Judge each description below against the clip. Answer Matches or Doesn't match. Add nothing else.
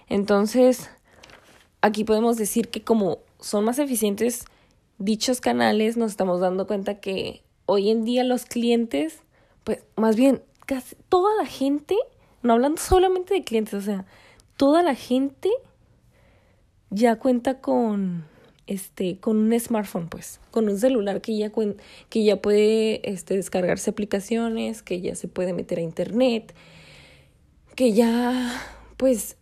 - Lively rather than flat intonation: Doesn't match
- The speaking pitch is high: Matches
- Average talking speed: Matches